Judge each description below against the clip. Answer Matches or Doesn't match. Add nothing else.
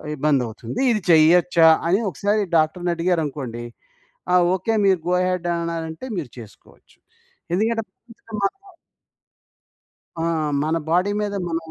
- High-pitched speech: Doesn't match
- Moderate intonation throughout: Matches